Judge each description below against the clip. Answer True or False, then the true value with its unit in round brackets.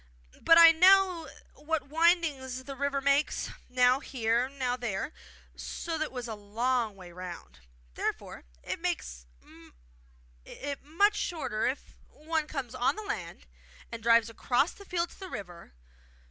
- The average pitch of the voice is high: True (265 Hz)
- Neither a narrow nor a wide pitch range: False (5.9 semitones)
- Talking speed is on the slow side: False (145 wpm)